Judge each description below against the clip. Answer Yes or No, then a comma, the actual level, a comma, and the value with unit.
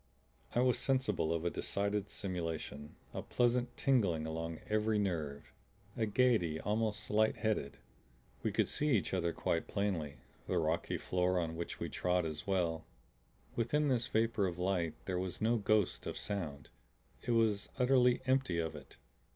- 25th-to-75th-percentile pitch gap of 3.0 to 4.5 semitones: No, wide, 5.4 semitones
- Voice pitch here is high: No, low, 100 Hz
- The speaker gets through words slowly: No, average, 160 wpm